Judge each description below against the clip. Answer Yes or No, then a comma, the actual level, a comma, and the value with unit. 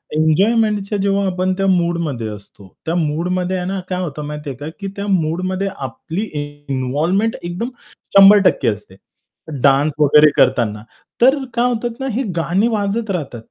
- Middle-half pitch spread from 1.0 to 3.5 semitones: No, average, 5.0 semitones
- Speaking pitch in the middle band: Yes, medium, 180 Hz